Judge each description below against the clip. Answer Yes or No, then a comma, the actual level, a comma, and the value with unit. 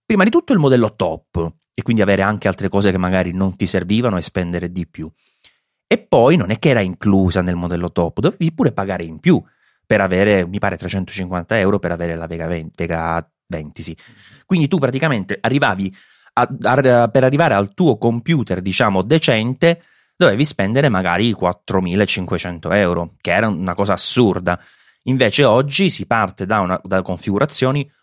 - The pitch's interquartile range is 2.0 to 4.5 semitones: No, wide, 5.5 semitones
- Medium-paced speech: No, fast, 175 wpm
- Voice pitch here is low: Yes, low, 100 Hz